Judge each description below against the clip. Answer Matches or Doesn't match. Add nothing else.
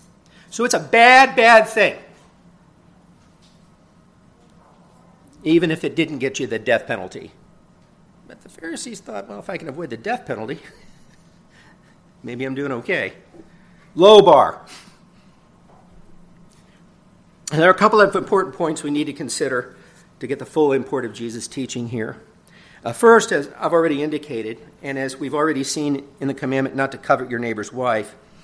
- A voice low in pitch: Doesn't match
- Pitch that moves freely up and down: Doesn't match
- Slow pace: Doesn't match